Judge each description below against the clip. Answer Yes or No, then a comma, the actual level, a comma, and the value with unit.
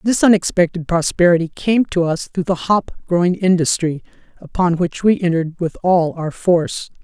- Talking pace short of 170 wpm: Yes, average, 160 wpm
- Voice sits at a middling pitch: Yes, medium, 175 Hz